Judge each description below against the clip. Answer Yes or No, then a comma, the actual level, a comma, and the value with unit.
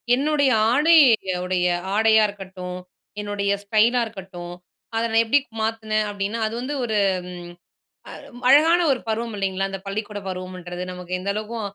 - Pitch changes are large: No, average, 3.3 semitones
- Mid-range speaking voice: No, high, 210 Hz